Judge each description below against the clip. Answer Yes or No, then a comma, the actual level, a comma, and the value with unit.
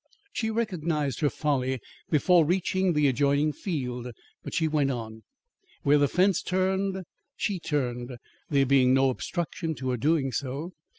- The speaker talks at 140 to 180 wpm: Yes, average, 145 wpm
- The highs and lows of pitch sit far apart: No, average, 5.0 semitones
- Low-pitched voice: No, medium, 150 Hz